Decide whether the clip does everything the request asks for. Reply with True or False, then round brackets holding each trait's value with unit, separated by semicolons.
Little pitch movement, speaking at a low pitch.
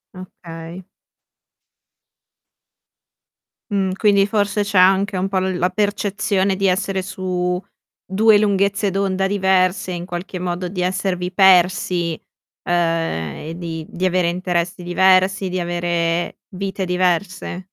False (1.7 semitones; 185 Hz)